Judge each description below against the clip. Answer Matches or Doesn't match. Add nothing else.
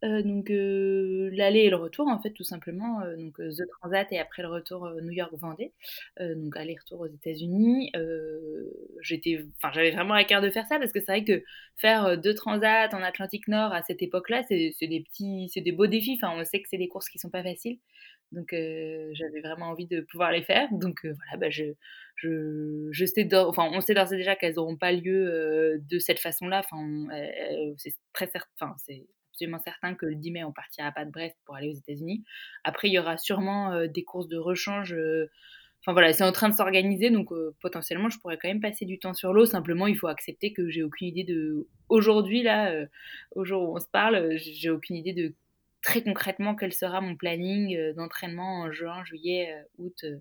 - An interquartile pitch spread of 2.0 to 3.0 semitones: Doesn't match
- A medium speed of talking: Doesn't match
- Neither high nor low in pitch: Matches